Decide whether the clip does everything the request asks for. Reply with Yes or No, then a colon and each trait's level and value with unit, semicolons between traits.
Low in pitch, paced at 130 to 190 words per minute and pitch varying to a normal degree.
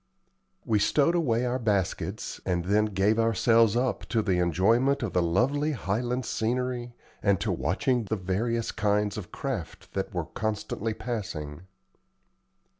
Yes: low, 110 Hz; average, 145 wpm; average, 3.9 semitones